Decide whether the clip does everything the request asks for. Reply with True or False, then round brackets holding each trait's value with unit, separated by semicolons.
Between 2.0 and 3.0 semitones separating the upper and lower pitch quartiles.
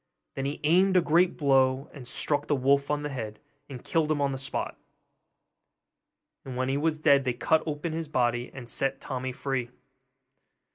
True (2.6 semitones)